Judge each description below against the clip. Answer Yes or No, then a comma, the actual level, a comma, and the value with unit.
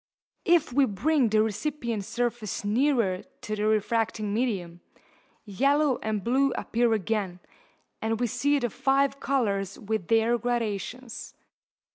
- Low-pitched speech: No, high, 230 Hz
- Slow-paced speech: Yes, slow, 125 wpm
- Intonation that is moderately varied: Yes, average, 3.9 semitones